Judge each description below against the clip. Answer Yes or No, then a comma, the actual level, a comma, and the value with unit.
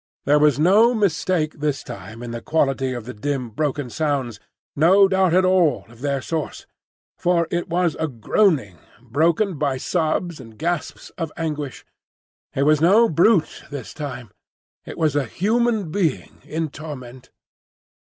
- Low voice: No, medium, 155 Hz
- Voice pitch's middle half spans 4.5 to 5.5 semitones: Yes, average, 4.8 semitones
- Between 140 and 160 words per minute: Yes, average, 150 wpm